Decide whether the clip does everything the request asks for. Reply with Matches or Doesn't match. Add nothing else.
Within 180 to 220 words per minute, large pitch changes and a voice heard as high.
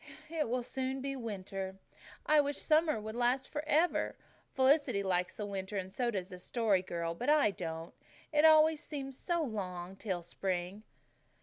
Doesn't match